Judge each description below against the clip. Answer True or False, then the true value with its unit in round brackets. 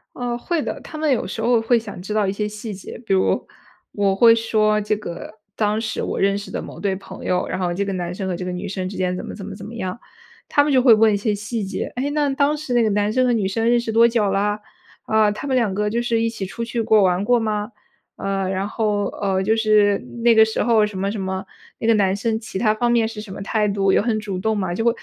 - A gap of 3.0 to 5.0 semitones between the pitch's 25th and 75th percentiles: False (2.6 semitones)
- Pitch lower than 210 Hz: False (215 Hz)